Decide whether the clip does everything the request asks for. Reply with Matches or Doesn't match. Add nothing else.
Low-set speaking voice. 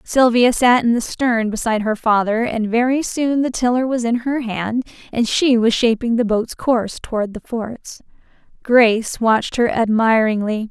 Doesn't match